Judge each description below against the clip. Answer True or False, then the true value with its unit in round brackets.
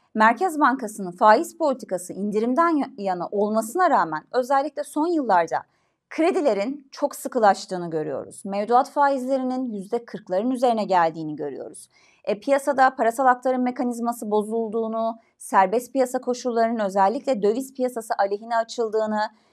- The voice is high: True (235 Hz)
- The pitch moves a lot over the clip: False (4.4 semitones)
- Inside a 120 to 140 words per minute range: False (110 wpm)